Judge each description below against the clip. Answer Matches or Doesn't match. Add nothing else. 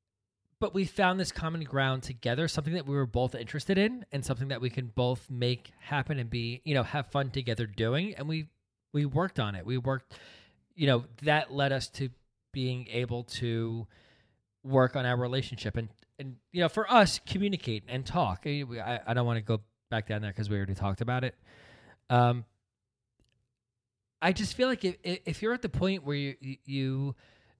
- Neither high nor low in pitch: Doesn't match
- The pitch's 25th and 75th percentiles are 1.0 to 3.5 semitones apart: Doesn't match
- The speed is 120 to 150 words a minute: Doesn't match